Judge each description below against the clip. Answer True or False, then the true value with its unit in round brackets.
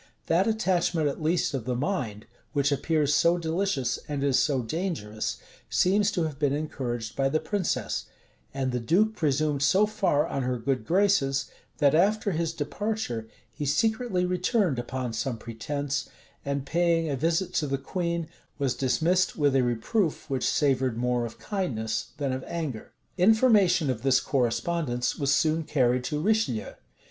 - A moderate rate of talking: True (160 wpm)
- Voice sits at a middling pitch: True (150 Hz)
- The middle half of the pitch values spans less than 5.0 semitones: False (5.3 semitones)